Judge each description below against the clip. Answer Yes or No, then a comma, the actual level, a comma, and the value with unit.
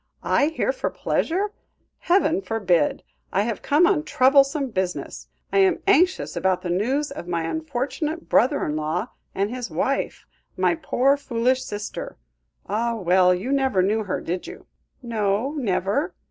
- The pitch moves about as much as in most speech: No, wide, 7.5 semitones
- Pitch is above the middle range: Yes, high, 245 Hz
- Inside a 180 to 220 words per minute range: No, average, 150 wpm